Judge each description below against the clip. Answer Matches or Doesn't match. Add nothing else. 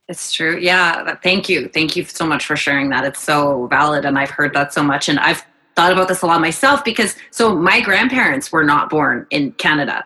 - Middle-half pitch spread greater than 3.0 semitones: Matches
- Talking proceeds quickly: Matches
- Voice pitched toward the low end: Doesn't match